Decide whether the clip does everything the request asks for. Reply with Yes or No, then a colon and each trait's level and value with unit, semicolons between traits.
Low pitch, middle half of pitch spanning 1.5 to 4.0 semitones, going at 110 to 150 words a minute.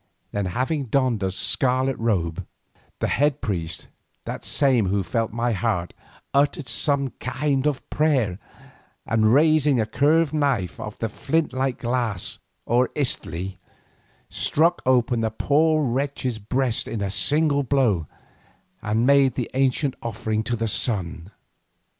No: low, 125 Hz; average, 4.6 semitones; average, 140 wpm